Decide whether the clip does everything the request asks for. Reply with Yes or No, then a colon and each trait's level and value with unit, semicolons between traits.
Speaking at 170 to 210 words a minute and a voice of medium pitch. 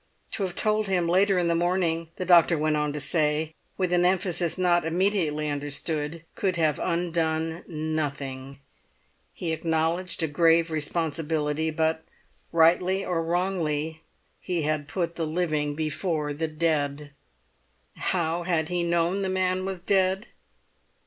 No: average, 140 wpm; medium, 165 Hz